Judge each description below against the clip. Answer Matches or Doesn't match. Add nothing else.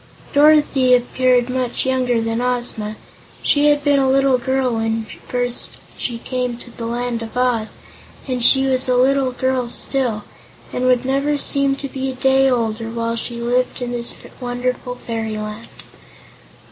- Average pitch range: Doesn't match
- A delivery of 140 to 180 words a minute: Matches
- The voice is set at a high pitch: Matches